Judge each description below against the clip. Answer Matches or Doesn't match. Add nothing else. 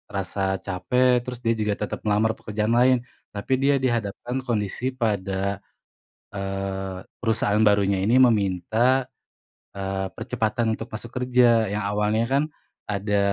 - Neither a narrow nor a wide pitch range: Matches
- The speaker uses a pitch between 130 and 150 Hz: Doesn't match